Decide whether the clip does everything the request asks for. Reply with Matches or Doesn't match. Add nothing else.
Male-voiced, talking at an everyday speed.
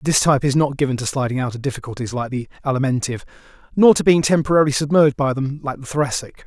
Doesn't match